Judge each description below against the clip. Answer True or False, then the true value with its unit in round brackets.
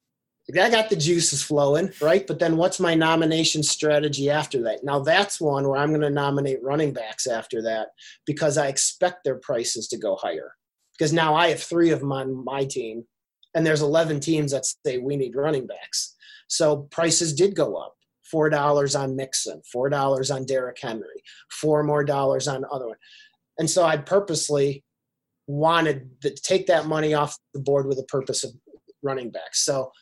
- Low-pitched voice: False (150 Hz)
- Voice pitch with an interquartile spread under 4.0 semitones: True (2.9 semitones)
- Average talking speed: True (190 wpm)